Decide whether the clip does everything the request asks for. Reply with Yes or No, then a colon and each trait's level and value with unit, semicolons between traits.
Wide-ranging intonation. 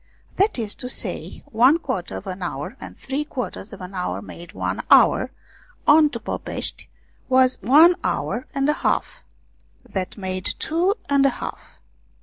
Yes: wide, 7.5 semitones